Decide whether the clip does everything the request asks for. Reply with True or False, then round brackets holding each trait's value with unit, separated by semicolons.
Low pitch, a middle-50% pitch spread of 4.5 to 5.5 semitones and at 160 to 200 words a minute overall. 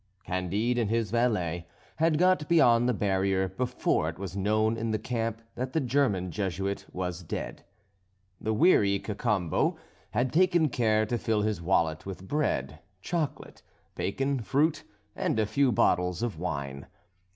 False (110 Hz; 5.0 semitones; 150 wpm)